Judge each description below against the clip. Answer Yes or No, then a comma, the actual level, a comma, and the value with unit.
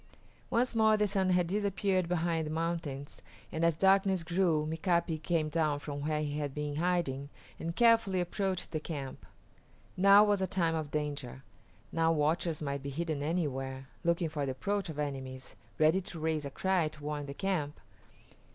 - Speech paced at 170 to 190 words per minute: Yes, average, 175 wpm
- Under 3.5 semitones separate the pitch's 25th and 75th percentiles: No, average, 3.9 semitones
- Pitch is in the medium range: Yes, medium, 160 Hz